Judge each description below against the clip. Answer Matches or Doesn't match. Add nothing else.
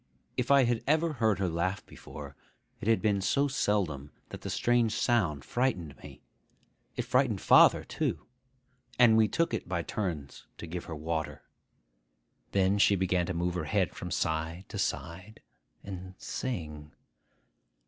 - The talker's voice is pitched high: Doesn't match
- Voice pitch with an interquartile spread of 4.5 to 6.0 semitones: Matches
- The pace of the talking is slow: Doesn't match